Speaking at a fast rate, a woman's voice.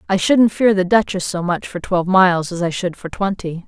Yes: fast, 245 wpm; female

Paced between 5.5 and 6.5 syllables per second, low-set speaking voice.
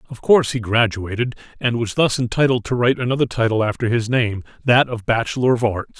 Yes: 6.1 syllables/s; low, 120 Hz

